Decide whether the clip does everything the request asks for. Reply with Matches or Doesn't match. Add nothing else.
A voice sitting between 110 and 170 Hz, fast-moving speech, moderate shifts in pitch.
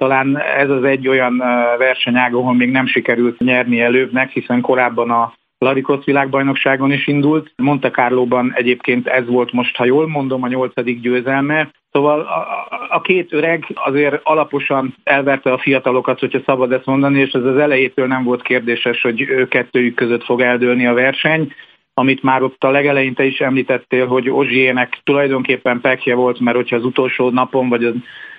Doesn't match